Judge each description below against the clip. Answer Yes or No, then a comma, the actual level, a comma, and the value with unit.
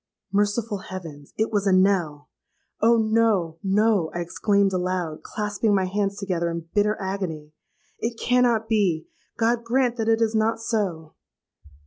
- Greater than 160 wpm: No, average, 140 wpm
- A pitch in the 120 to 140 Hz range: No, high, 200 Hz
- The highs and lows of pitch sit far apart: No, average, 3.8 semitones